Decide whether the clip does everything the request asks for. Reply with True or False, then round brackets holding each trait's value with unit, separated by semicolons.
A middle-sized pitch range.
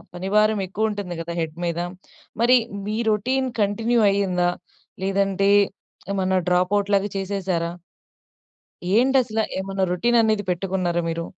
True (3.0 semitones)